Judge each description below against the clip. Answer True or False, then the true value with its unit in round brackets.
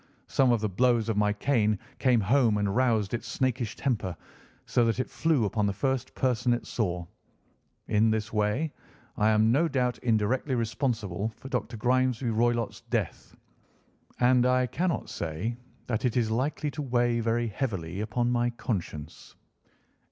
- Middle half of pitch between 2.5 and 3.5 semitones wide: True (3.1 semitones)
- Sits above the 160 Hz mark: False (120 Hz)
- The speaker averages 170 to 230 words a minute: False (160 wpm)